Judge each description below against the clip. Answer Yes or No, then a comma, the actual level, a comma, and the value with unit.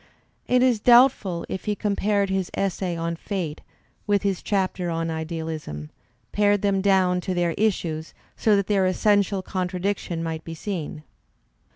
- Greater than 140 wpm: Yes, average, 150 wpm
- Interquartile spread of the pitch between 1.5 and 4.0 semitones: Yes, average, 3.4 semitones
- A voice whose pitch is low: No, medium, 185 Hz